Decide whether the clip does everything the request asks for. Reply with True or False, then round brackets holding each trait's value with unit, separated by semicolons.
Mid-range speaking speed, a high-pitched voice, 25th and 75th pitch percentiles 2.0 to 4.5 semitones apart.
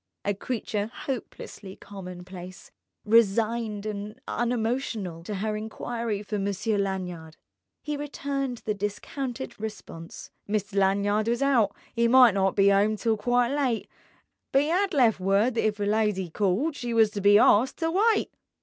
True (150 wpm; 215 Hz; 3.4 semitones)